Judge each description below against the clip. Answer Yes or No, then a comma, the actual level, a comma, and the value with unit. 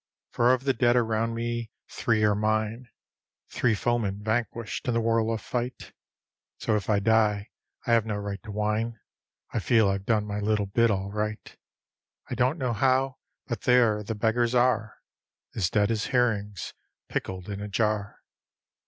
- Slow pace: No, average, 170 wpm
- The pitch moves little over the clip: Yes, narrow, 2.3 semitones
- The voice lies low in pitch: Yes, low, 110 Hz